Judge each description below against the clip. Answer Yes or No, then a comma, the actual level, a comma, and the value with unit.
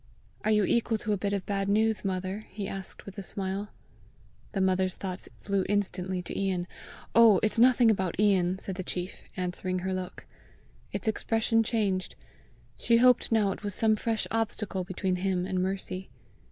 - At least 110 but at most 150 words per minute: No, average, 175 wpm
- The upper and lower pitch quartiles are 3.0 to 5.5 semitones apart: No, narrow, 2.5 semitones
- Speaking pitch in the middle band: No, high, 195 Hz